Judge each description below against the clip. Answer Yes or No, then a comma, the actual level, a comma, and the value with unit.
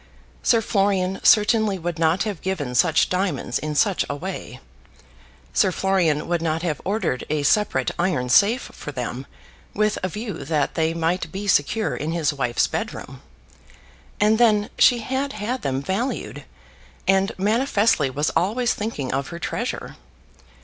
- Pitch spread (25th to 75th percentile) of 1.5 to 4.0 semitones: No, wide, 5.6 semitones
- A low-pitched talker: No, medium, 185 Hz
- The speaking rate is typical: Yes, average, 155 wpm